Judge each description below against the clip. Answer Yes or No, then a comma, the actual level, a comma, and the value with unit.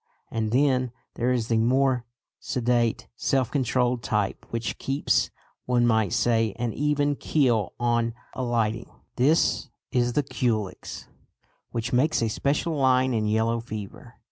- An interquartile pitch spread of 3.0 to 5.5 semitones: No, narrow, 2.4 semitones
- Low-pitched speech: Yes, low, 120 Hz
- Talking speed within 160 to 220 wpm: No, slow, 135 wpm